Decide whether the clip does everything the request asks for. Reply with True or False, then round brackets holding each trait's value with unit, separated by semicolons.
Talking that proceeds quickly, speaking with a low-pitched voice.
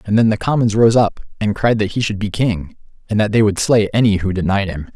True (265 wpm; 105 Hz)